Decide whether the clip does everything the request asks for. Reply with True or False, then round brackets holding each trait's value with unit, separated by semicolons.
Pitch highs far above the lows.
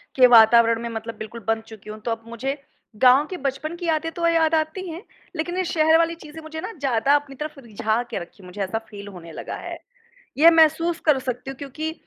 True (5.9 semitones)